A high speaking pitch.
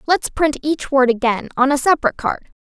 Yes: very high, 275 Hz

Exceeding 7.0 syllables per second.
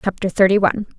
Yes: 7.5 syllables/s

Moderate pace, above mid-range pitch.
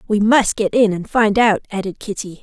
No: fast, 225 wpm; high, 210 Hz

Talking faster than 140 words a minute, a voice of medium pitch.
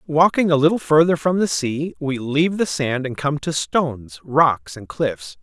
Yes: average, 200 wpm; medium, 150 Hz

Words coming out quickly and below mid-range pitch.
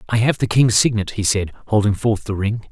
Yes: fast, 245 wpm; low, 105 Hz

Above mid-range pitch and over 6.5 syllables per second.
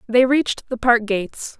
No: high, 235 Hz; 5.1 syllables/s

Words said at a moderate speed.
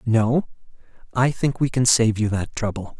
Yes: average, 180 wpm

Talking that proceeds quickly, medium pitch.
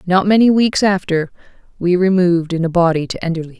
No: average, 185 wpm; medium, 180 Hz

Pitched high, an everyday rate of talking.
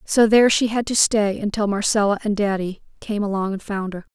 No: high, 205 Hz; fast, 215 wpm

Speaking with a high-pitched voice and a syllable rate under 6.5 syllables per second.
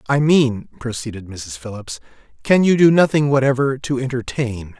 No: low, 130 Hz; 4.9 syllables/s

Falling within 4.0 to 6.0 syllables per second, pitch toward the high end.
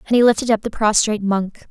No: 6.5 syllables/s; high, 215 Hz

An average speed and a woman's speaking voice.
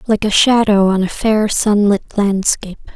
Yes: average, 165 wpm; female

